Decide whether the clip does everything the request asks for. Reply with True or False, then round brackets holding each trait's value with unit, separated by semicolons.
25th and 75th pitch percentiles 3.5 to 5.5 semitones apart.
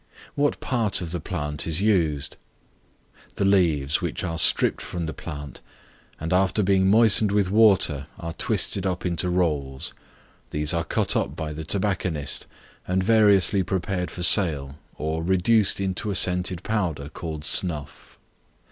True (4.0 semitones)